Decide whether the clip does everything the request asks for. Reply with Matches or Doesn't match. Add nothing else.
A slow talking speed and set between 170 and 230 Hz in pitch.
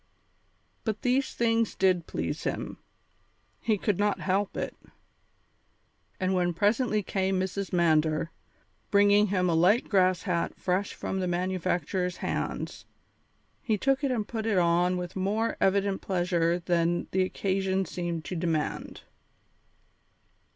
Matches